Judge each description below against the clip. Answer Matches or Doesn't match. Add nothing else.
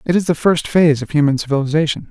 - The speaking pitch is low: Doesn't match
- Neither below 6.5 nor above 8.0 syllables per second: Matches